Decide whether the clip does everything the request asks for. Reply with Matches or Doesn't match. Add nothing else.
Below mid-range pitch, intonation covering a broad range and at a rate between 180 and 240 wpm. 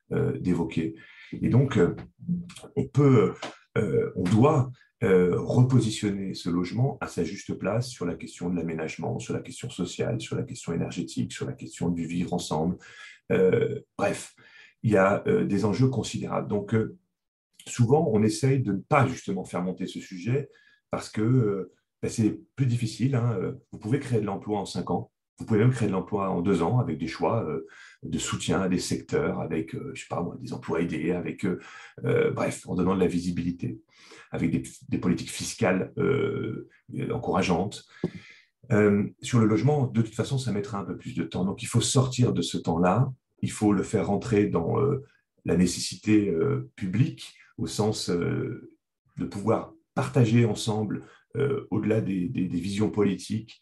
Doesn't match